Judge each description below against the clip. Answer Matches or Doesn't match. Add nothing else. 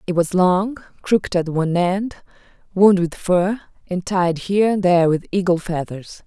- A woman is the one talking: Matches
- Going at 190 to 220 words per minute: Doesn't match